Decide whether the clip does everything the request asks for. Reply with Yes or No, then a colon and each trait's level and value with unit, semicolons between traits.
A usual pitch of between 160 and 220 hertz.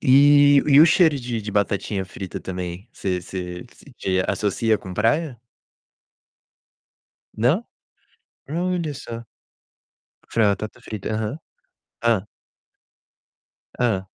No: low, 110 Hz